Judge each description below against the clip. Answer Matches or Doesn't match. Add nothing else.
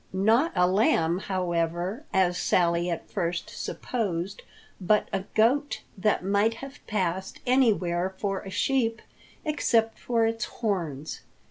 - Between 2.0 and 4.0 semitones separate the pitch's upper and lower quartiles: Doesn't match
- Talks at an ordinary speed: Doesn't match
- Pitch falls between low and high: Doesn't match